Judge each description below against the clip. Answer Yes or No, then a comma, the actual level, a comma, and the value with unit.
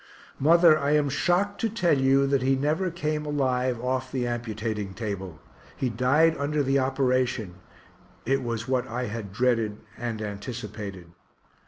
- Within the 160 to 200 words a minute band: No, average, 150 wpm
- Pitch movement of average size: Yes, average, 4.1 semitones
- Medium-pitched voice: No, low, 130 Hz